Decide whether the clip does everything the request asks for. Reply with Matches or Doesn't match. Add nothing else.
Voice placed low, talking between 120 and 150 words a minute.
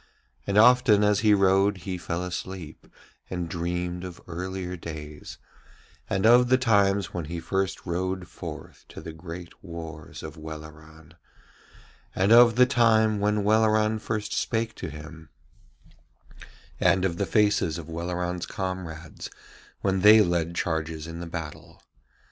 Matches